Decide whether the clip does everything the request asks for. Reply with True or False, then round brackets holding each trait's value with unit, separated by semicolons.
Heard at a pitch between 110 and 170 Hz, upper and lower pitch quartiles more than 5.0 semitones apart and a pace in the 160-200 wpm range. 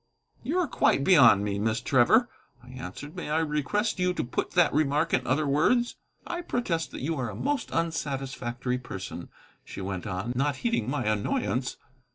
True (140 Hz; 5.6 semitones; 180 wpm)